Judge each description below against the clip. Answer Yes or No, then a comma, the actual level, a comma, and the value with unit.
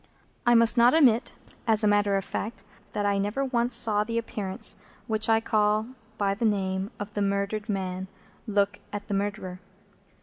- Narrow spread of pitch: Yes, narrow, 2.1 semitones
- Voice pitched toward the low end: No, high, 210 Hz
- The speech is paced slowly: No, average, 175 wpm